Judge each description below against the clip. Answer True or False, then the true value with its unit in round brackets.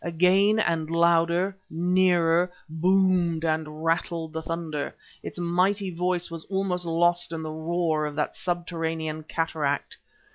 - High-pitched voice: False (170 Hz)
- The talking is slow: True (130 wpm)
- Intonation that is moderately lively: False (1.9 semitones)